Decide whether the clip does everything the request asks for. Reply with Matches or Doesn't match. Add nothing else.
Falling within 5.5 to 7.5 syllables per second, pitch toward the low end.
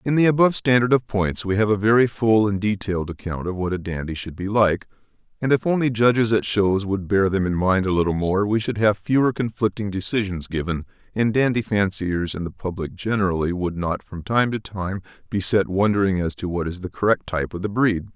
Matches